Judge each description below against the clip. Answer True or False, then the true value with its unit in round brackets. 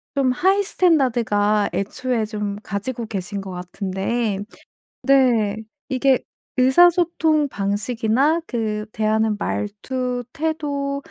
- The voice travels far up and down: False (4.9 semitones)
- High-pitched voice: True (240 Hz)